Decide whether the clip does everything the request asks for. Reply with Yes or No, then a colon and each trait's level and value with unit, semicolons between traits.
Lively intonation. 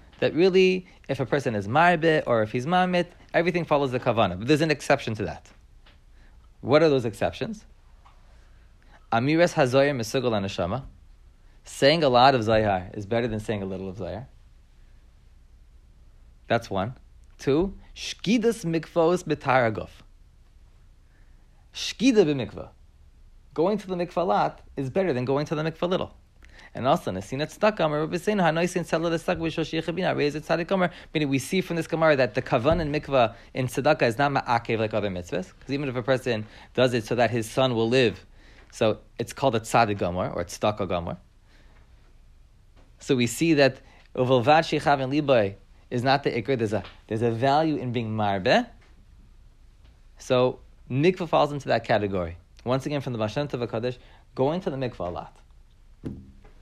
Yes: wide, 7.4 semitones